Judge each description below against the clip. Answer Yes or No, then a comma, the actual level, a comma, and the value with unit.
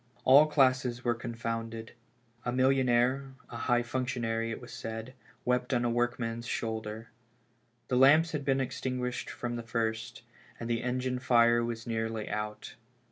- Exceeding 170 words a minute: No, average, 145 wpm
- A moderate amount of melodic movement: No, narrow, 2.0 semitones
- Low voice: Yes, low, 120 Hz